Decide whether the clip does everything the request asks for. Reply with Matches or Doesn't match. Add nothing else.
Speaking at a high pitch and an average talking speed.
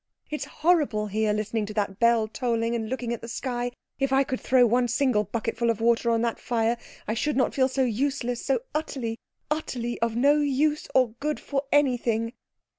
Matches